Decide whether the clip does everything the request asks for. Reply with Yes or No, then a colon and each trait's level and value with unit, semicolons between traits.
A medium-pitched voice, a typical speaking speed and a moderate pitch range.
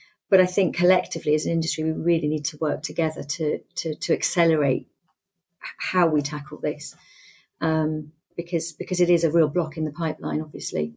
No: medium, 160 Hz; average, 180 wpm; narrow, 2.1 semitones